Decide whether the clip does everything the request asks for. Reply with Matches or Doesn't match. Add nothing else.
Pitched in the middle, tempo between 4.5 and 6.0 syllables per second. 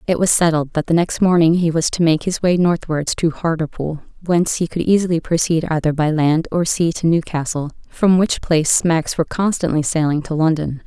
Matches